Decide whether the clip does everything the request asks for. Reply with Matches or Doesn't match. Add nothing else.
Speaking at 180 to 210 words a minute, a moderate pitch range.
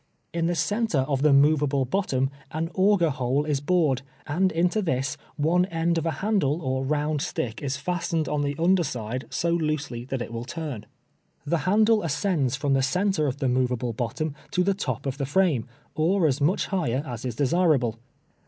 Matches